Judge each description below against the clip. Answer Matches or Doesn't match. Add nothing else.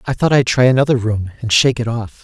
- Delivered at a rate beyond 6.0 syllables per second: Matches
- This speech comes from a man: Matches